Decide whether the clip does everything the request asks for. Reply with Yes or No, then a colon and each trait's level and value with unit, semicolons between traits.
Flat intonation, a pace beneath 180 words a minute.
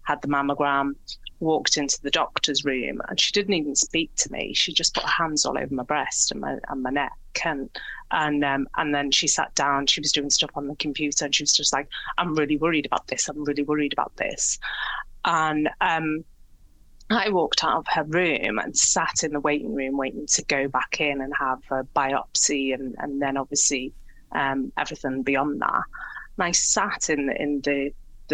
No: narrow, 1.6 semitones; fast, 205 wpm